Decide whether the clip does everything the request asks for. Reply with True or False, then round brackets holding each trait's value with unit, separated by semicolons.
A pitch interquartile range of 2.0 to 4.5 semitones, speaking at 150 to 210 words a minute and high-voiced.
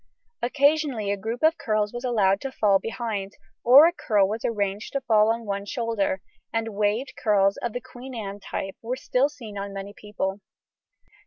True (3.7 semitones; 180 wpm; 220 Hz)